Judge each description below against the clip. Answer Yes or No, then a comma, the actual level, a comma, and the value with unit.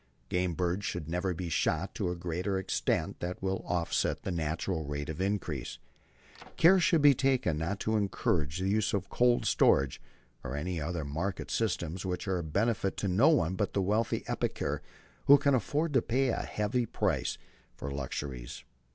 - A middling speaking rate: Yes, average, 175 wpm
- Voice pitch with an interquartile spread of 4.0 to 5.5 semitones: Yes, average, 4.7 semitones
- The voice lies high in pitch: No, very low, 95 Hz